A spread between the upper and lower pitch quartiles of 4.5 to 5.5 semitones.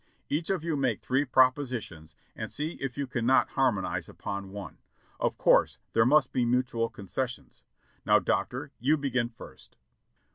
No: average, 3.4 semitones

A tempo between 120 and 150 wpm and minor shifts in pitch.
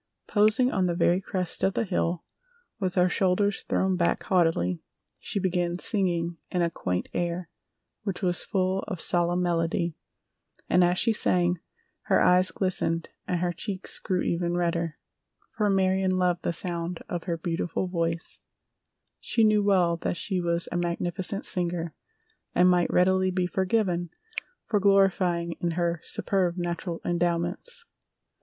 Yes: average, 145 wpm; narrow, 1.7 semitones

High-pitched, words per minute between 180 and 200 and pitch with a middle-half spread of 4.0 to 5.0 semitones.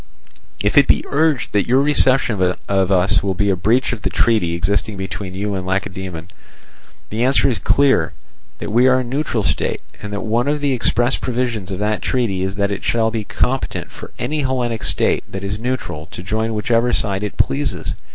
No: low, 105 Hz; average, 195 wpm; average, 4.6 semitones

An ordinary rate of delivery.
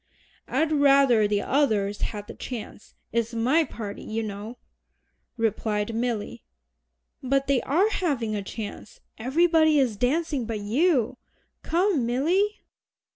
No: slow, 125 wpm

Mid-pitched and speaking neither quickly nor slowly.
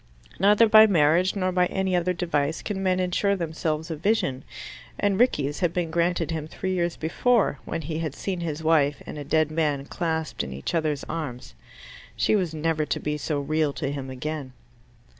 Yes: medium, 160 Hz; average, 190 wpm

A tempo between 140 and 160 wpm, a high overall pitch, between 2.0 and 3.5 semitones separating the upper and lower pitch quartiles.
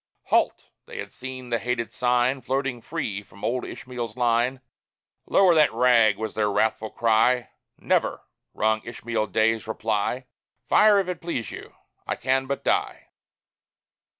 No: average, 145 wpm; low, 120 Hz; average, 2.9 semitones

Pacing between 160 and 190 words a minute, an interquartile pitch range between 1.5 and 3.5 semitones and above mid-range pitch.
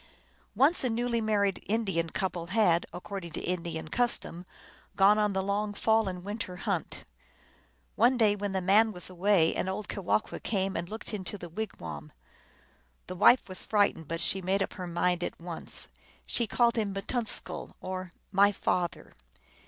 Yes: average, 175 wpm; average, 3.2 semitones; high, 195 Hz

